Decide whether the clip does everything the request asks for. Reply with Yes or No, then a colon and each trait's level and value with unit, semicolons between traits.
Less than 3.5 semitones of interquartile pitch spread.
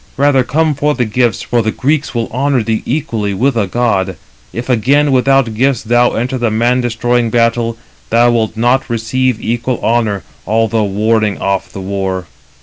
Yes: average, 2.7 semitones